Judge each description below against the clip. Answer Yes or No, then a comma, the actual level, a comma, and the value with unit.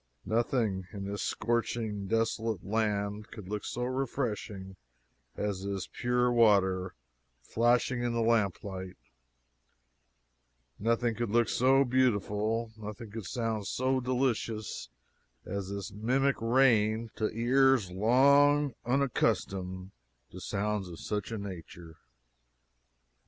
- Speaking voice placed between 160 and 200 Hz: No, low, 110 Hz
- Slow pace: Yes, slow, 110 wpm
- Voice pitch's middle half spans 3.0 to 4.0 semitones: Yes, average, 3.3 semitones